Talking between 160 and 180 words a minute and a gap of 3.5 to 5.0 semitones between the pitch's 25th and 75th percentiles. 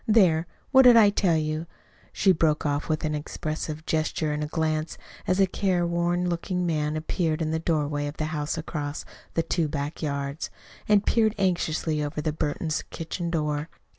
No: average, 175 wpm; narrow, 2.5 semitones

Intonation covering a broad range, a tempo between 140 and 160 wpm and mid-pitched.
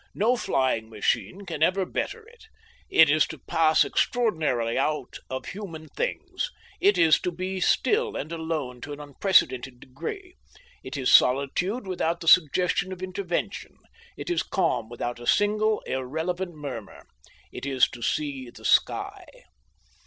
Yes: wide, 6.3 semitones; average, 145 wpm; medium, 160 Hz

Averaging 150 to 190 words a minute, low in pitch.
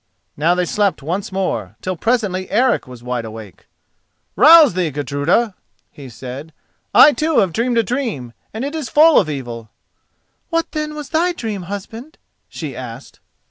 No: average, 160 wpm; medium, 185 Hz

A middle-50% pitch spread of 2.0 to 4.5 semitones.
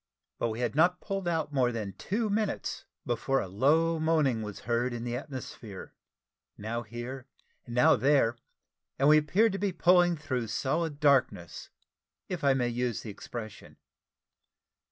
No: wide, 5.6 semitones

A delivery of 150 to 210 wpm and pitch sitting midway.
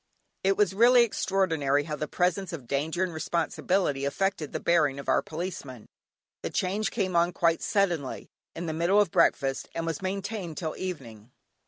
Yes: average, 170 wpm; medium, 170 Hz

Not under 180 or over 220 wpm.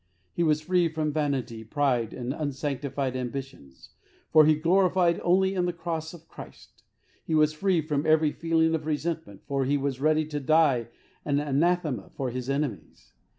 No: average, 165 wpm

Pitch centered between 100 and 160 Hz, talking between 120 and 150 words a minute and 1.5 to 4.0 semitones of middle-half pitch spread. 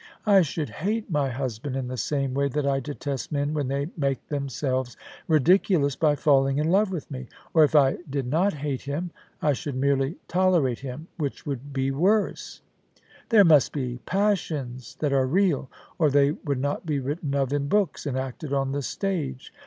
No: medium, 140 Hz; average, 190 wpm; average, 2.9 semitones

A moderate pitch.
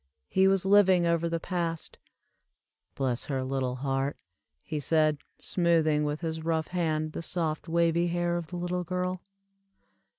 Yes: medium, 165 Hz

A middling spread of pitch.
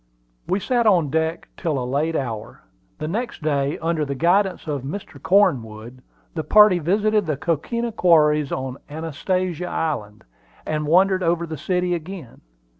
Yes: average, 4.3 semitones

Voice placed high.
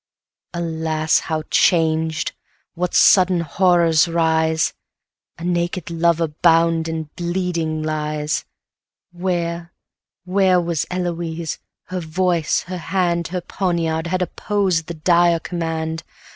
No: medium, 170 Hz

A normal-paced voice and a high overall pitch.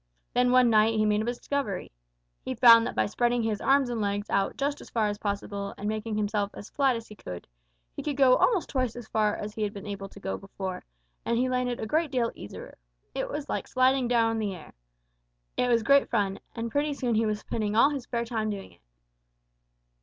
No: fast, 230 wpm; high, 225 Hz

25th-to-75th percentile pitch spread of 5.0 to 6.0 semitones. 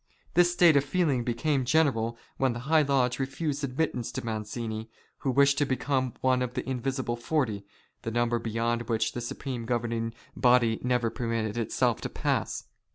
No: average, 2.9 semitones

